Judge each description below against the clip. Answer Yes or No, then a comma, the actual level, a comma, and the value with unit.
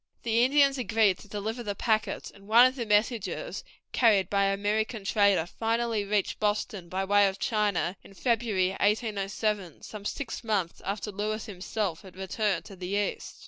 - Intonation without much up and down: Yes, narrow, 2.3 semitones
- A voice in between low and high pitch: No, high, 210 Hz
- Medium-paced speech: Yes, average, 170 wpm